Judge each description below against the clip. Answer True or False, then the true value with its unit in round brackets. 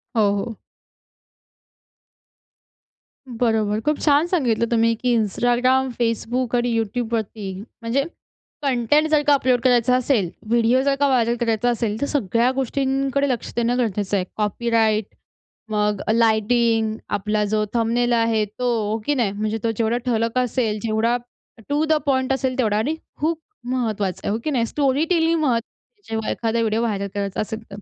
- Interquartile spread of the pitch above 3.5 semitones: False (2.9 semitones)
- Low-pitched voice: False (235 Hz)